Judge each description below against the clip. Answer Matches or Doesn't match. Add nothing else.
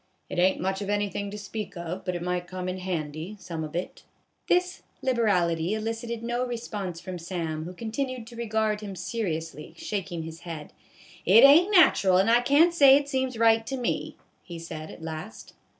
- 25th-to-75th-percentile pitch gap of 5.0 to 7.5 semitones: Matches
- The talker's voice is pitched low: Doesn't match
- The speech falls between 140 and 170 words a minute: Doesn't match